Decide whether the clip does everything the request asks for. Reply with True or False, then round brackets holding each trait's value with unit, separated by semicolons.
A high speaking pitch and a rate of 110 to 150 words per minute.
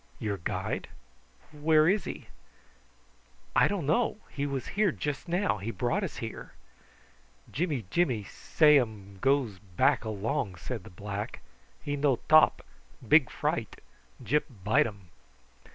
False (135 Hz; 135 wpm)